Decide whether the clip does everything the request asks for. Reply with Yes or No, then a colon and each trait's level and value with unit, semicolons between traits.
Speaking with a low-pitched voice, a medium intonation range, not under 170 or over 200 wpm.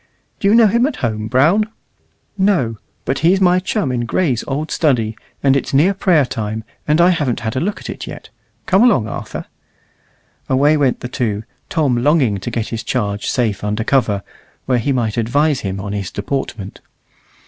No: low, 130 Hz; wide, 6.5 semitones; average, 185 wpm